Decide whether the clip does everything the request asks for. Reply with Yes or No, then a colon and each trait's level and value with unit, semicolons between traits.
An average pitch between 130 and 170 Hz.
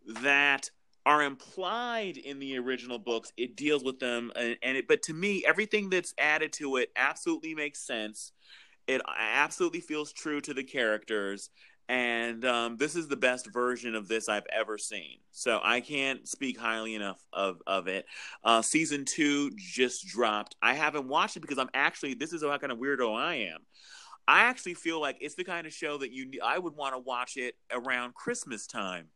Yes: medium, 140 Hz